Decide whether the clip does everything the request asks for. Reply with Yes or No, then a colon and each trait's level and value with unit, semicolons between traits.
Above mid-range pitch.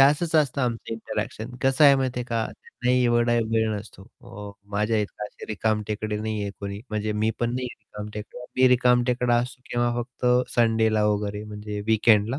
No: low, 115 Hz